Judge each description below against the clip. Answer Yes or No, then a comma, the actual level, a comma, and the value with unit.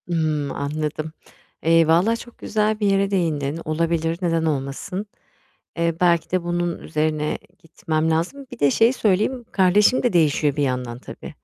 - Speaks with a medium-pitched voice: Yes, medium, 165 Hz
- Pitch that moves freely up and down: No, average, 3.7 semitones